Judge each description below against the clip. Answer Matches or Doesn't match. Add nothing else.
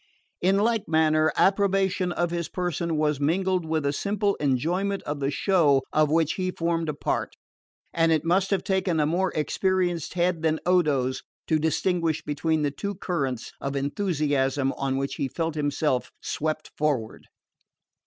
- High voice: Doesn't match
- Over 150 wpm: Matches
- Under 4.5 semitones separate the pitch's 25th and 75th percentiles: Matches